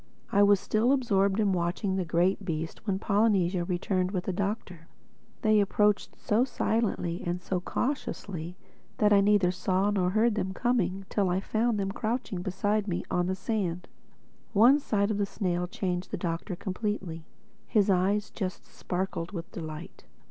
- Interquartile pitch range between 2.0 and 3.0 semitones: Yes, average, 2.7 semitones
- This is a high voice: Yes, high, 195 Hz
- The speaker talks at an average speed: Yes, average, 165 wpm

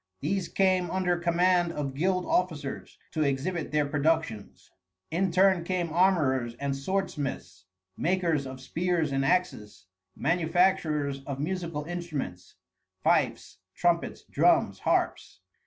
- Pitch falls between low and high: Yes, medium, 165 Hz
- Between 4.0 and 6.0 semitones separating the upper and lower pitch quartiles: Yes, average, 4.4 semitones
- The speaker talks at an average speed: No, slow, 115 wpm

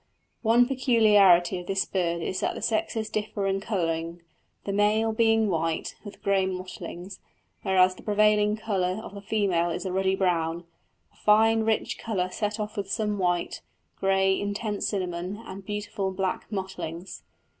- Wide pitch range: No, narrow, 2.5 semitones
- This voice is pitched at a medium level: No, high, 195 Hz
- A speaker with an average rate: Yes, average, 155 wpm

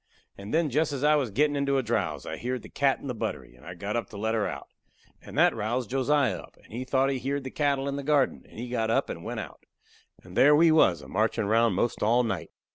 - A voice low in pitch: Yes, low, 125 Hz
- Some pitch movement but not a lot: Yes, average, 4.3 semitones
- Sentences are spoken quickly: Yes, fast, 270 wpm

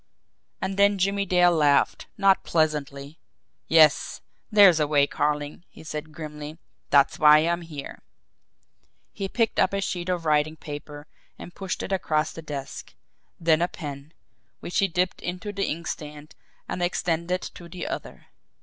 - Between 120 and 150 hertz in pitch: No, medium, 165 Hz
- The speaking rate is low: No, average, 150 wpm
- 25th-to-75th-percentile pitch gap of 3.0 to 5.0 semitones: Yes, average, 3.4 semitones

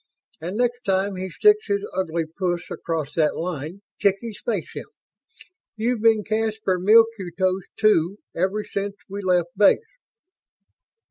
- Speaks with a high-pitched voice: Yes, high, 195 Hz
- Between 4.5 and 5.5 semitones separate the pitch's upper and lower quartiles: No, average, 3.8 semitones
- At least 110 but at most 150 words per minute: Yes, slow, 135 wpm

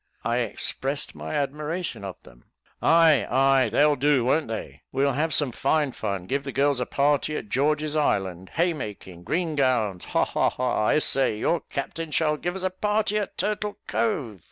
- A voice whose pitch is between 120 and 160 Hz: Yes, medium, 140 Hz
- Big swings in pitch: No, average, 4.7 semitones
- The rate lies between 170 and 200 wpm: Yes, average, 180 wpm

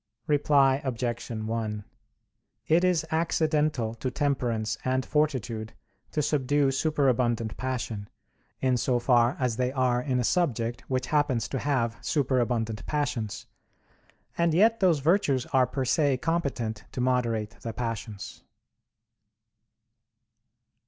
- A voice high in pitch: No, low, 130 Hz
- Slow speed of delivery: Yes, slow, 120 wpm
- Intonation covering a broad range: No, average, 3.9 semitones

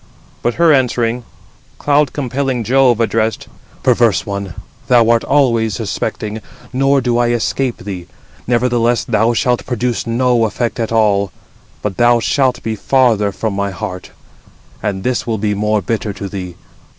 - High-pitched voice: No, low, 115 Hz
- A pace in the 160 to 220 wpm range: No, average, 150 wpm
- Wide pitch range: No, average, 3.0 semitones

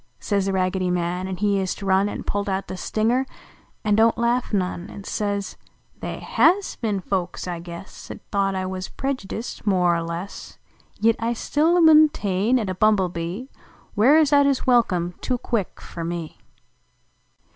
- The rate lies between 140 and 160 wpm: No, average, 170 wpm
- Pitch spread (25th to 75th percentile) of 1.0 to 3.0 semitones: No, average, 4.2 semitones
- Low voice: No, high, 200 Hz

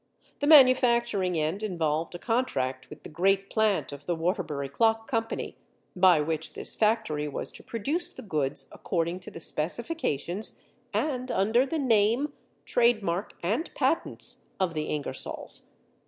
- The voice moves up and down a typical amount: No, wide, 6.7 semitones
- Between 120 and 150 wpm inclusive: Yes, average, 145 wpm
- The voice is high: Yes, high, 195 Hz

